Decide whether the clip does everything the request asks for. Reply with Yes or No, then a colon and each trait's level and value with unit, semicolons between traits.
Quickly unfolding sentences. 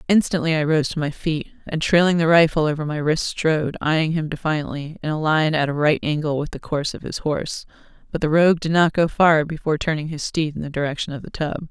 Yes: fast, 240 wpm